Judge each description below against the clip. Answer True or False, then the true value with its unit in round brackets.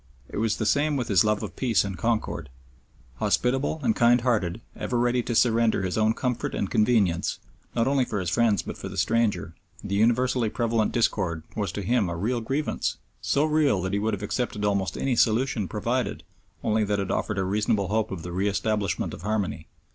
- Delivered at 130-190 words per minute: False (200 wpm)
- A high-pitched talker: False (110 Hz)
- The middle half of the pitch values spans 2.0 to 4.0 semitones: True (3.5 semitones)